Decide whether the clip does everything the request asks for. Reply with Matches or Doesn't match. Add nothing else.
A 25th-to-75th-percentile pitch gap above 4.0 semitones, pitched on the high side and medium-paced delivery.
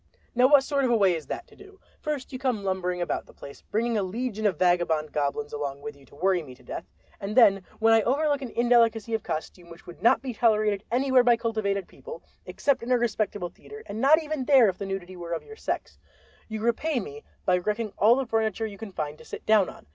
Doesn't match